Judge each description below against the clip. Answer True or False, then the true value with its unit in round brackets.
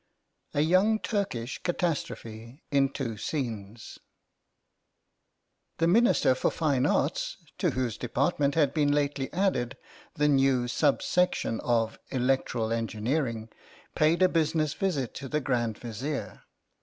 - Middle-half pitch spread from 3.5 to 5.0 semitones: True (4.7 semitones)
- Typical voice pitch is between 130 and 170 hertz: True (135 Hz)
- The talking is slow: True (120 wpm)